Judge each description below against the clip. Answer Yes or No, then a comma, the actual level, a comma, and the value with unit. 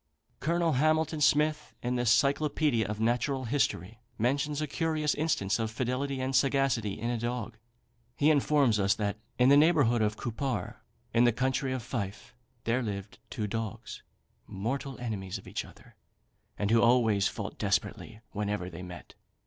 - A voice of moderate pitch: No, low, 120 Hz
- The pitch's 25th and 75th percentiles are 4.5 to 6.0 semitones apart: Yes, average, 4.8 semitones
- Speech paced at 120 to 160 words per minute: Yes, average, 155 wpm